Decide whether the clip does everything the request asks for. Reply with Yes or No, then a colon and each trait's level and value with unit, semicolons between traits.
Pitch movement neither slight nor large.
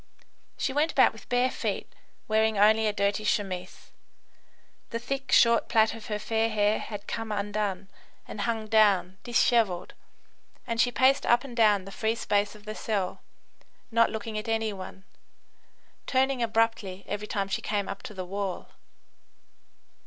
No: narrow, 2.3 semitones